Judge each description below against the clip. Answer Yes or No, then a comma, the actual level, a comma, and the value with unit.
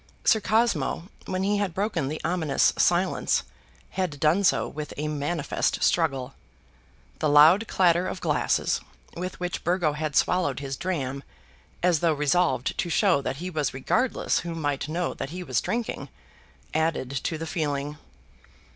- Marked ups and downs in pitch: No, average, 3.9 semitones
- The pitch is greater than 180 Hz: No, medium, 160 Hz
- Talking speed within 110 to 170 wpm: Yes, average, 155 wpm